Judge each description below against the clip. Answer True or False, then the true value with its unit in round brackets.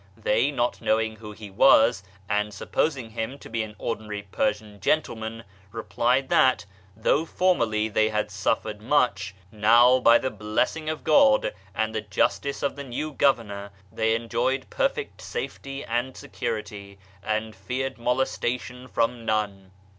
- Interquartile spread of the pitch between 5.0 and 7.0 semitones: False (3.5 semitones)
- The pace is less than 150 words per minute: True (140 wpm)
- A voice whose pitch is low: True (115 Hz)